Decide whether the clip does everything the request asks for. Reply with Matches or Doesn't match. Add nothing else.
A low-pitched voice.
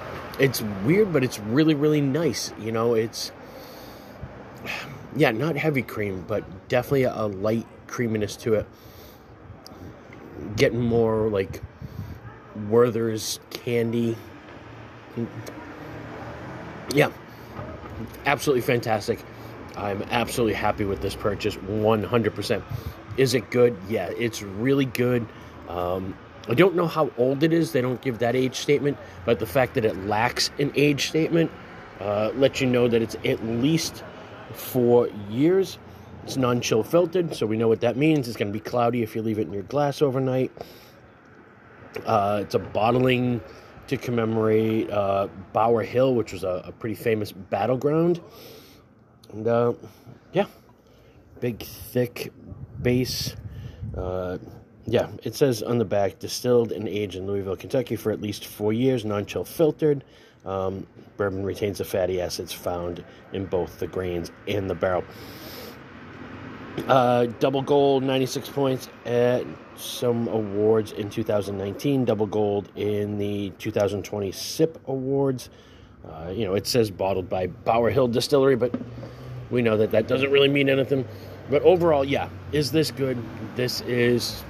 Matches